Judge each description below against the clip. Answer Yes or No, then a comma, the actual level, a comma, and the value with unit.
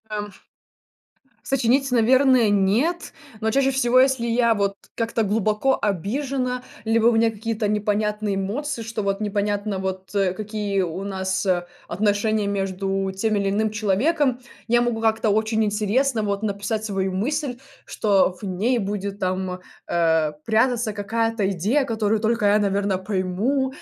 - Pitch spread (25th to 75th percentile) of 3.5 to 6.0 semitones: No, average, 2.9 semitones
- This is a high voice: Yes, high, 215 Hz